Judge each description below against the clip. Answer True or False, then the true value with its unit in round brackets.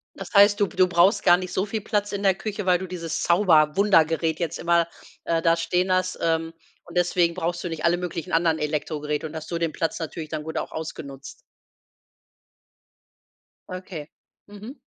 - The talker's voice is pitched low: False (170 Hz)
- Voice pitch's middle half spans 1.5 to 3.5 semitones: True (2.4 semitones)